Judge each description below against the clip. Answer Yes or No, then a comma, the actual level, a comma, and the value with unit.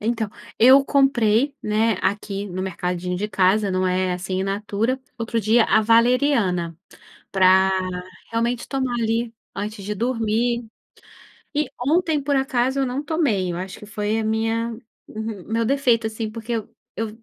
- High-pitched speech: Yes, high, 225 Hz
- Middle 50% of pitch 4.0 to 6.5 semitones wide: No, average, 3.3 semitones